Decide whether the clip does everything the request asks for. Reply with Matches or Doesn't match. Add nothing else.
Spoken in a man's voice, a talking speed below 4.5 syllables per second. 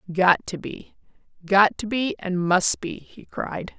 Doesn't match